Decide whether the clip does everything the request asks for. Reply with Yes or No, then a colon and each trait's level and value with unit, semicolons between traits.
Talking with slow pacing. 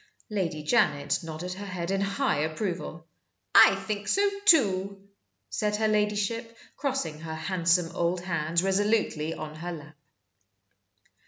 Yes: slow, 130 wpm